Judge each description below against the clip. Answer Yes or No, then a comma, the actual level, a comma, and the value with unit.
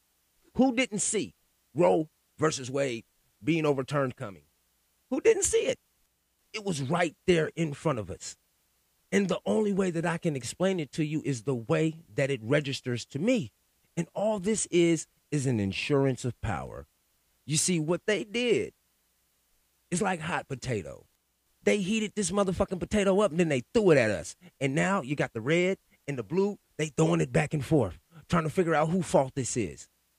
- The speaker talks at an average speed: Yes, average, 185 wpm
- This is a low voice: No, medium, 160 Hz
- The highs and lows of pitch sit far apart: Yes, wide, 5.9 semitones